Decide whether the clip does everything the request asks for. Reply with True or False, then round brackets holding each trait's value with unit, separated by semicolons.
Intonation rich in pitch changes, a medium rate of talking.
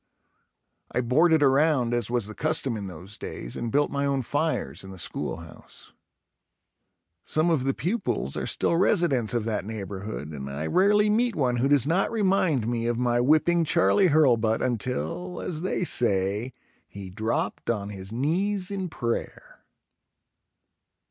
True (7.2 semitones; 155 wpm)